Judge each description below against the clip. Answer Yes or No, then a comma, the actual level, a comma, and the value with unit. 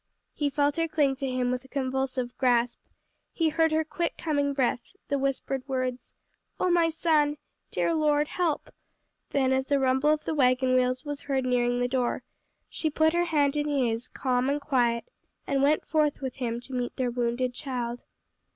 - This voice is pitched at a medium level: No, very high, 270 Hz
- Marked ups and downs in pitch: No, average, 2.9 semitones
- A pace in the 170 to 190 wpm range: Yes, average, 185 wpm